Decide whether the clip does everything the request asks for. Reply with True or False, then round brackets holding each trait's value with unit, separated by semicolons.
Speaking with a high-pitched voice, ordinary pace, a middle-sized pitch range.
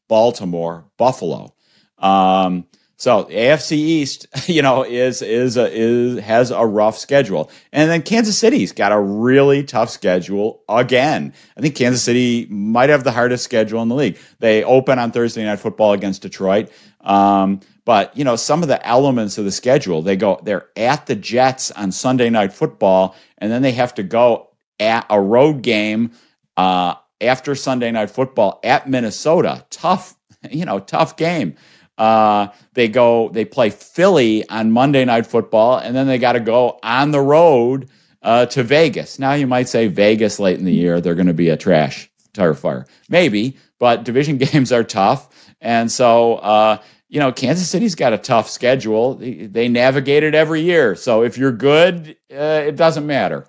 False (120 Hz; 180 wpm; 4.2 semitones)